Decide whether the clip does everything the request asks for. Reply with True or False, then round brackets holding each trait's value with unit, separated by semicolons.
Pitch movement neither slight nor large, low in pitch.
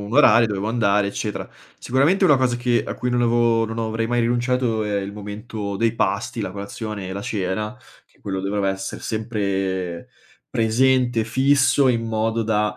True (3.0 semitones; 110 Hz)